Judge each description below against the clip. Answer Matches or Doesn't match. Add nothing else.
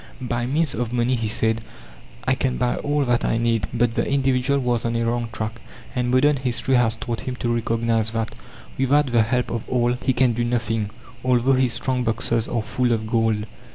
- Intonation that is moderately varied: Doesn't match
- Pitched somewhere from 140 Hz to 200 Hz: Doesn't match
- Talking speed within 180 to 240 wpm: Matches